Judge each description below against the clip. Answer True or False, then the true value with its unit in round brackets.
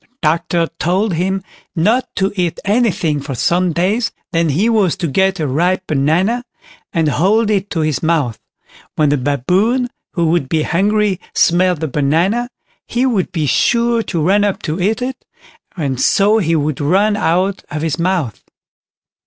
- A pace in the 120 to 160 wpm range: False (170 wpm)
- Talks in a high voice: False (180 Hz)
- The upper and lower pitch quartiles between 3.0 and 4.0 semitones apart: False (4.7 semitones)